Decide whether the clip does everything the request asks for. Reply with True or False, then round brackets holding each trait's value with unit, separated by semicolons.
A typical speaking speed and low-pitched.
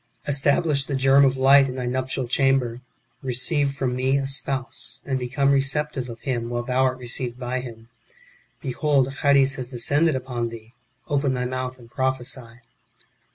True (160 wpm; 130 Hz)